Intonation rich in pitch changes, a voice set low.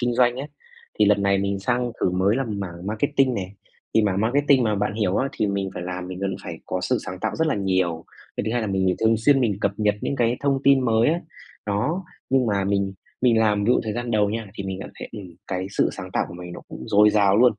No: average, 3.9 semitones; low, 105 Hz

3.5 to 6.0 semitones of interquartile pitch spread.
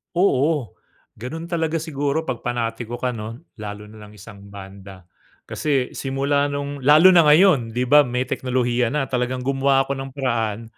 Yes: average, 4.0 semitones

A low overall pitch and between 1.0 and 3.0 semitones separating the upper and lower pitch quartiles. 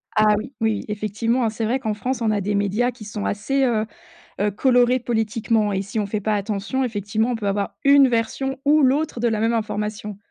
No: high, 220 Hz; average, 2.7 semitones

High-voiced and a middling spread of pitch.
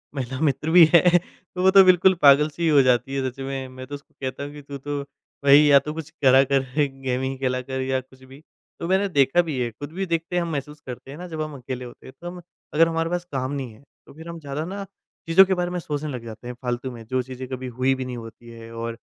No: medium, 140 Hz; average, 4.0 semitones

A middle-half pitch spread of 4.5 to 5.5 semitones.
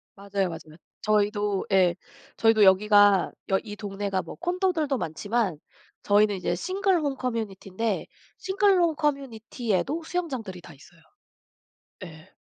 No: wide, 6.4 semitones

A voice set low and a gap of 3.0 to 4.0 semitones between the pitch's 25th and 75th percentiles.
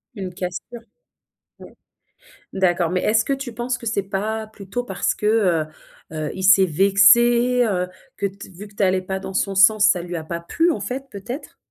No: high, 200 Hz; average, 3.6 semitones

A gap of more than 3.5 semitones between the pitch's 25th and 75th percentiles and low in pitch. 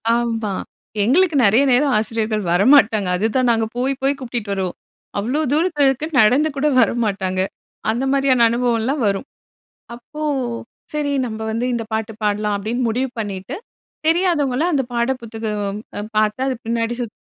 No: average, 4.1 semitones; high, 235 Hz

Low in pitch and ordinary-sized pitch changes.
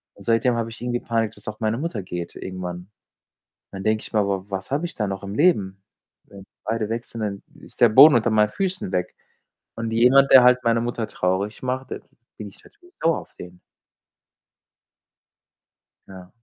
Yes: low, 110 Hz; average, 4.0 semitones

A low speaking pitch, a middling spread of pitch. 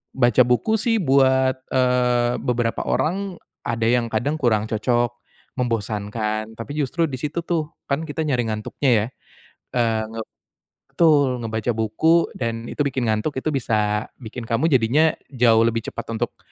Yes: low, 120 Hz; average, 4.0 semitones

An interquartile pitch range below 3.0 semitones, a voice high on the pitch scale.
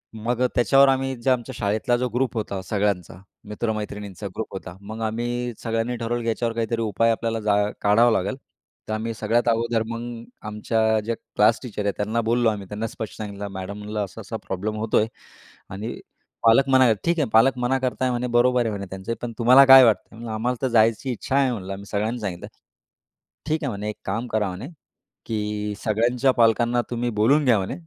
No: narrow, 2.5 semitones; low, 115 Hz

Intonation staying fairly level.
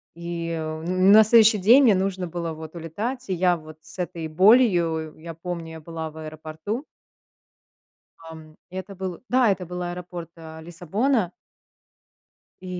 No: average, 3.2 semitones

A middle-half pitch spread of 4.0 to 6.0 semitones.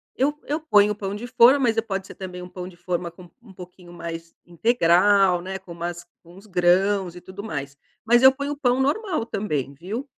Yes: average, 5.0 semitones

